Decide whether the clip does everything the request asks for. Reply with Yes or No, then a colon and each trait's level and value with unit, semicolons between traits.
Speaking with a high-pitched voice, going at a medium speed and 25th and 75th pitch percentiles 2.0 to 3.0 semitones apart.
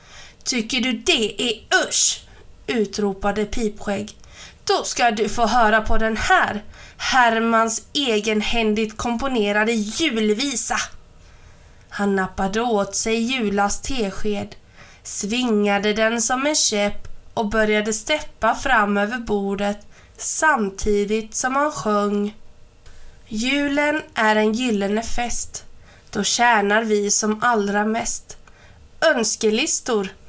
No: high, 220 Hz; slow, 105 wpm; narrow, 2.6 semitones